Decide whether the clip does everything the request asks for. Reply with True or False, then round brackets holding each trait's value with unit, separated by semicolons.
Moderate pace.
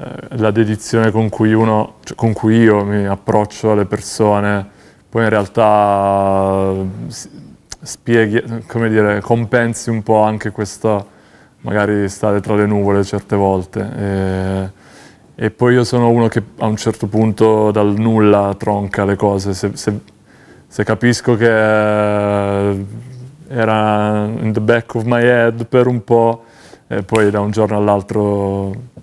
True (140 wpm)